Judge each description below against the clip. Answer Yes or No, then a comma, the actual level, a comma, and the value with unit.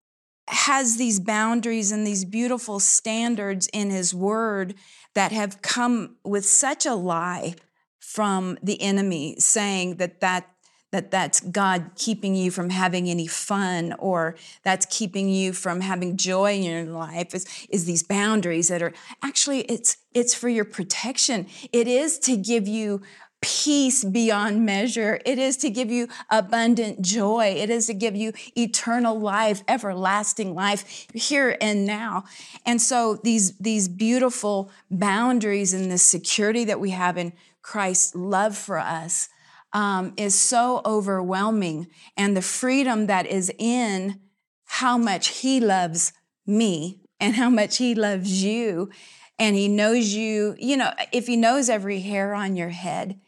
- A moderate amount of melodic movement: Yes, average, 3.5 semitones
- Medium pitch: No, high, 205 Hz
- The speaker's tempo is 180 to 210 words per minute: No, average, 150 wpm